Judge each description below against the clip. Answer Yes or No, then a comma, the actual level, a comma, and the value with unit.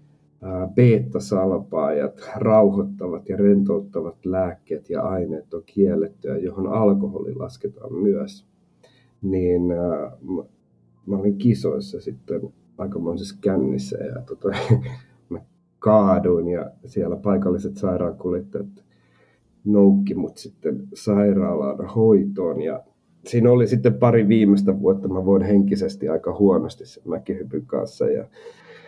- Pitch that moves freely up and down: No, average, 4.0 semitones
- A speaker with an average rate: Yes, average, 105 wpm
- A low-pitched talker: Yes, low, 100 Hz